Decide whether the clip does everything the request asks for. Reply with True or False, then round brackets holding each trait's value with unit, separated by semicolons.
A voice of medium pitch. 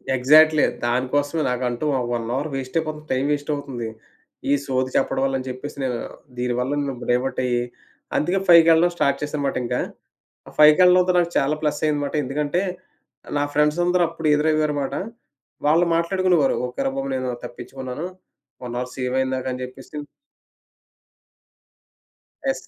True (145 Hz)